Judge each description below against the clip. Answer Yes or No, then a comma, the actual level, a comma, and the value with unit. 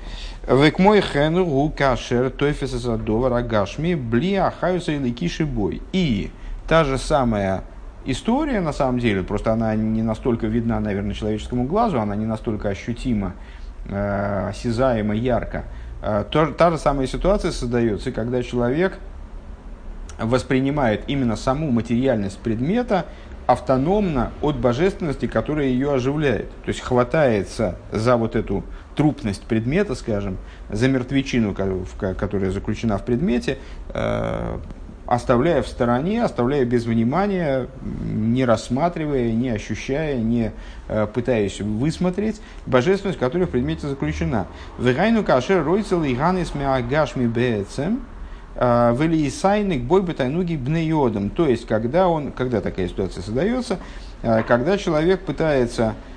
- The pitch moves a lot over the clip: Yes, wide, 6.1 semitones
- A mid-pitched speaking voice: No, low, 125 Hz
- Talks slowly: Yes, slow, 105 wpm